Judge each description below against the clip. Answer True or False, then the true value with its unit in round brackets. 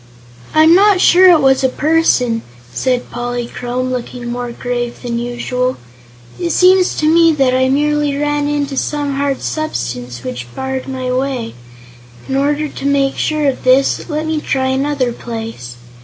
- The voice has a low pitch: False (265 Hz)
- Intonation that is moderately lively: True (3.4 semitones)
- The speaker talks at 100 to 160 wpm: True (155 wpm)